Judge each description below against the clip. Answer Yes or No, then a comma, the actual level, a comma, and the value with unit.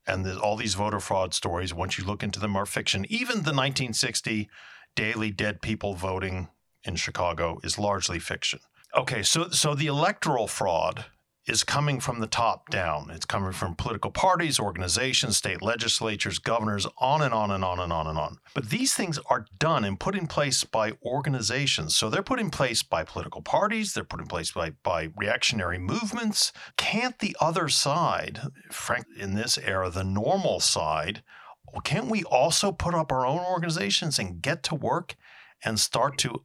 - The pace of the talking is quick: No, average, 180 wpm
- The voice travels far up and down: Yes, wide, 7.6 semitones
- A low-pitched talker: Yes, low, 115 Hz